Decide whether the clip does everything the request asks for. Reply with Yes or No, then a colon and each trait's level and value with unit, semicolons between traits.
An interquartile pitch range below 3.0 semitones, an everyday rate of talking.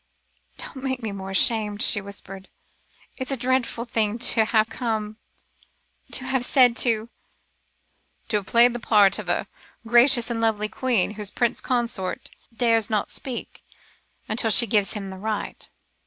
Yes: narrow, 2.5 semitones; average, 155 wpm